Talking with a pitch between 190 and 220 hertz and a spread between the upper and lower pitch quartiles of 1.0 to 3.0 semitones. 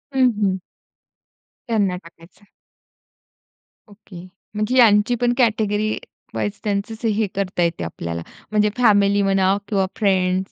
Yes: high, 205 Hz; narrow, 2.4 semitones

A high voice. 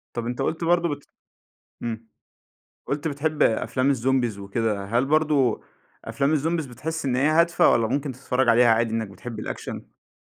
No: low, 130 Hz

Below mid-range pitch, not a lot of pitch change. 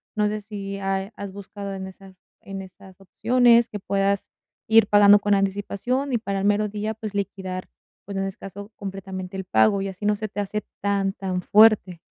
No: high, 200 Hz; narrow, 1.4 semitones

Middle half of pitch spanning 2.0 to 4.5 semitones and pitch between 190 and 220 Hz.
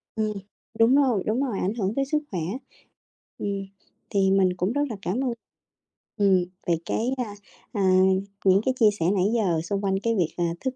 Yes: average, 3.9 semitones; high, 205 Hz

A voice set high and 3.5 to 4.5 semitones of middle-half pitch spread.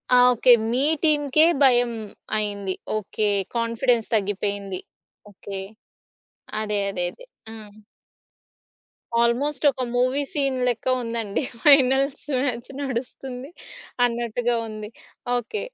Yes: high, 240 Hz; average, 3.9 semitones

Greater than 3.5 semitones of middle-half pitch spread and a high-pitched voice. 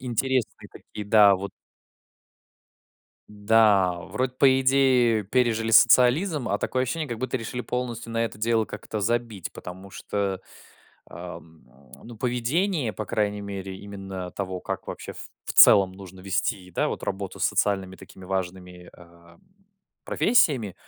No: average, 4.4 semitones; low, 105 Hz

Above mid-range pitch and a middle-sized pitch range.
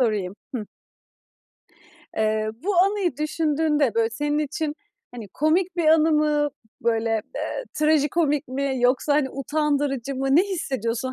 Yes: very high, 290 Hz; average, 4.1 semitones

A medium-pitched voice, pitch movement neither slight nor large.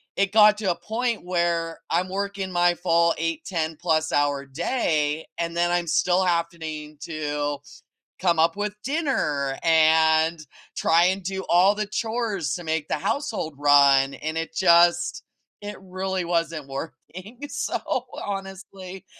Yes: medium, 170 Hz; average, 3.3 semitones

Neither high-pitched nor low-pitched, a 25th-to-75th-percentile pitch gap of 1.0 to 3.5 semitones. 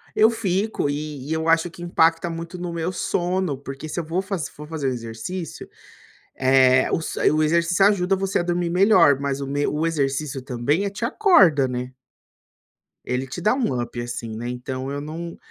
No: medium, 160 Hz; average, 4.7 semitones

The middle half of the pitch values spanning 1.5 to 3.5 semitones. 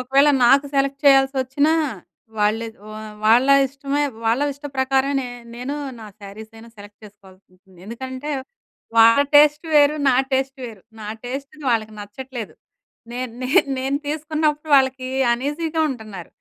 No: average, 4.0 semitones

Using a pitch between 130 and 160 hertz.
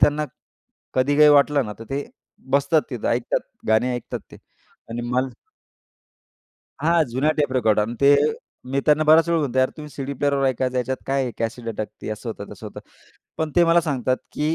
Yes: low, 135 Hz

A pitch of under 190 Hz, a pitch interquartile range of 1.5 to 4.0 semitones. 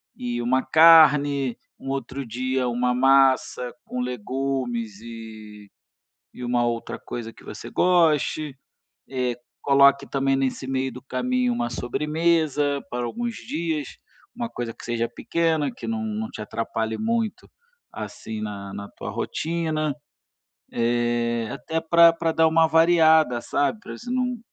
No: low, 135 Hz; average, 5.0 semitones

